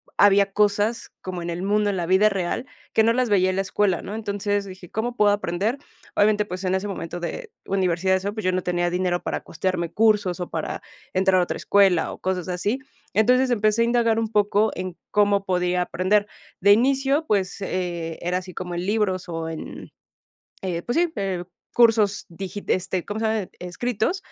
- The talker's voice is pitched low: No, high, 195 Hz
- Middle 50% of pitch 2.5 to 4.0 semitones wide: Yes, average, 2.8 semitones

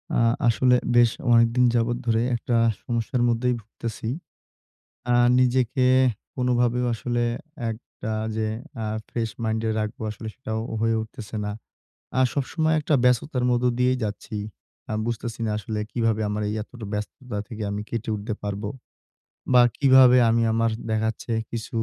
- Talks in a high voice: No, low, 115 Hz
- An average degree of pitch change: No, narrow, 2.2 semitones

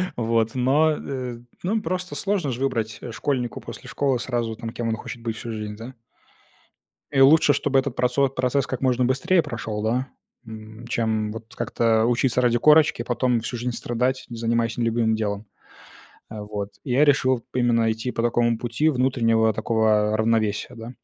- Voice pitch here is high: No, low, 120 Hz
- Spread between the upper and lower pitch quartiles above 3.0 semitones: No, average, 2.7 semitones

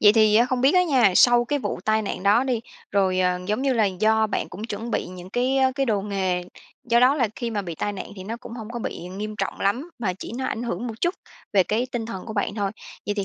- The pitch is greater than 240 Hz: No, high, 220 Hz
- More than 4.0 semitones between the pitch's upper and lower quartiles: No, average, 3.5 semitones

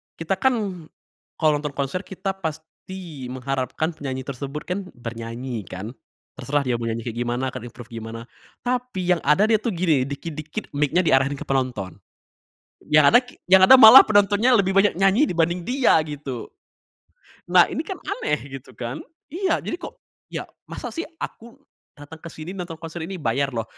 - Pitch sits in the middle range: Yes, medium, 155 Hz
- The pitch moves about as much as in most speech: No, wide, 6.6 semitones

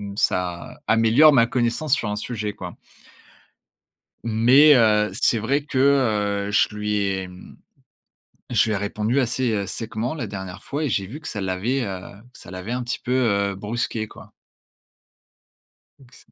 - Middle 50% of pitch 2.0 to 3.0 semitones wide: No, average, 3.8 semitones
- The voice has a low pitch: Yes, low, 110 Hz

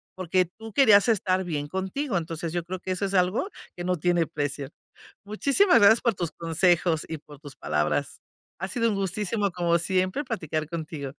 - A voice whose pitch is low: No, medium, 180 Hz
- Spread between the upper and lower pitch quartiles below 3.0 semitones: No, average, 3.8 semitones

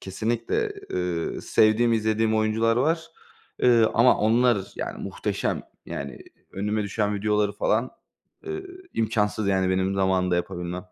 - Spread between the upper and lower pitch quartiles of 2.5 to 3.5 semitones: Yes, average, 3.2 semitones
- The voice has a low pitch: Yes, low, 105 Hz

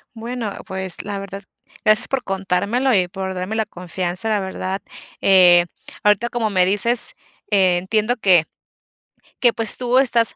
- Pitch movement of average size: Yes, average, 3.3 semitones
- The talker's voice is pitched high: Yes, high, 200 Hz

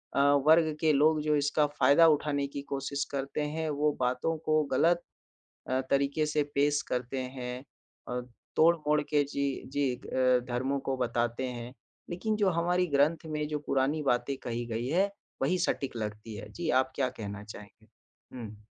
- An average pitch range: Yes, average, 3.6 semitones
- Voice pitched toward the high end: No, medium, 140 Hz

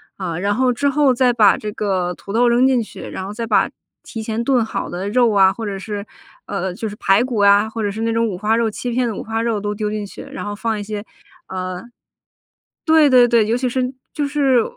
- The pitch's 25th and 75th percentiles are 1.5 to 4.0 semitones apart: Yes, average, 3.1 semitones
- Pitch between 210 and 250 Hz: Yes, high, 220 Hz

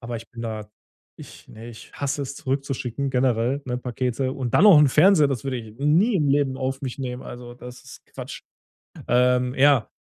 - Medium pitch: No, low, 130 Hz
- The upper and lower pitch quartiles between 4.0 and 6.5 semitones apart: No, narrow, 2.4 semitones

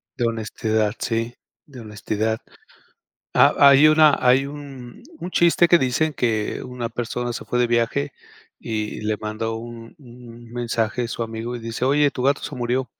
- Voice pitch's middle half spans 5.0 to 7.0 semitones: No, narrow, 2.6 semitones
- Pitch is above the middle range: No, low, 120 Hz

